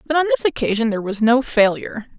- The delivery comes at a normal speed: No, fast, 220 wpm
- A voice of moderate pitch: No, very high, 255 Hz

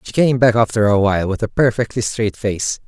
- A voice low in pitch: Yes, low, 110 Hz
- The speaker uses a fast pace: Yes, fast, 230 wpm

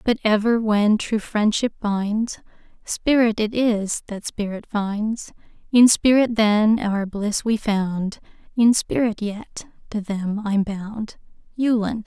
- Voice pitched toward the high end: Yes, high, 215 Hz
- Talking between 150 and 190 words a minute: No, slow, 135 wpm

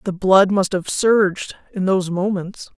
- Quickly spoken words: No, average, 170 wpm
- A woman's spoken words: Yes, female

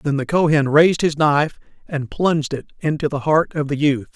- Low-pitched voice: No, medium, 150 Hz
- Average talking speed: No, fast, 215 wpm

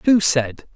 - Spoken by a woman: No, male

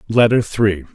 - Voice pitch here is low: Yes, low, 105 Hz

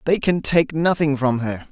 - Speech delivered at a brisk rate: Yes, fast, 210 wpm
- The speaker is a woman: No, male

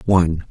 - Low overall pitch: Yes, very low, 85 Hz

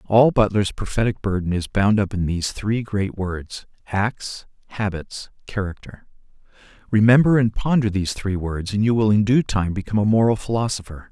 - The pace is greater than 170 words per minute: No, average, 160 wpm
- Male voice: Yes, male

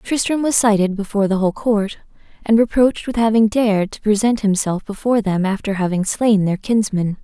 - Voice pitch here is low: No, high, 210 Hz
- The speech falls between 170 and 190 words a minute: Yes, average, 180 wpm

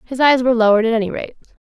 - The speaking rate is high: Yes, fast, 260 wpm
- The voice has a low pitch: No, high, 240 Hz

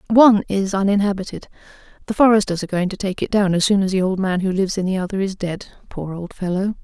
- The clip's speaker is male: No, female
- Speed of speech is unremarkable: No, fast, 235 wpm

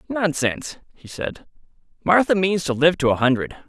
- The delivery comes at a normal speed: Yes, average, 165 wpm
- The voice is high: No, medium, 155 Hz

